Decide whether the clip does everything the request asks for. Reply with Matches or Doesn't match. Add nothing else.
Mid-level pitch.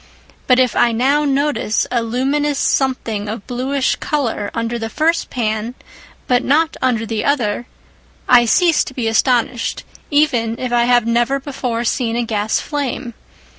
Doesn't match